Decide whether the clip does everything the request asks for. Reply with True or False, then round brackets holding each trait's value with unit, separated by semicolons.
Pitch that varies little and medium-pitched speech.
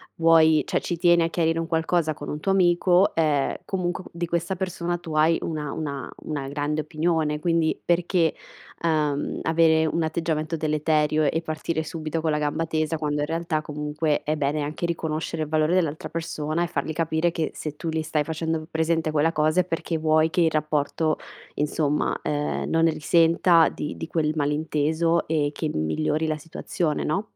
True (1.6 semitones; 160 Hz)